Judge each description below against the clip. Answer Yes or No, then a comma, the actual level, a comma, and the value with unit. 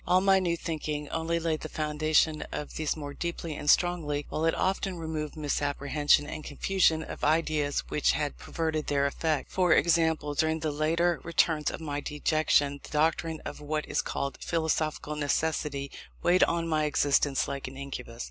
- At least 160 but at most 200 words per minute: Yes, average, 170 wpm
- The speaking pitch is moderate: Yes, medium, 155 Hz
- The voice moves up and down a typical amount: No, narrow, 2.0 semitones